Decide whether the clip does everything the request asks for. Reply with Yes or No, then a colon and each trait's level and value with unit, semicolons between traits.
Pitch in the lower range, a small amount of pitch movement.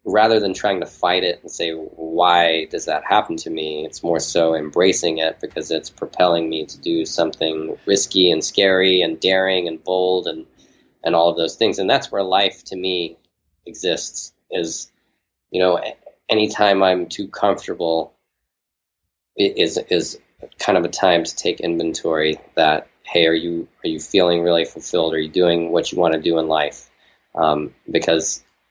Yes: very low, 85 Hz; narrow, 2.2 semitones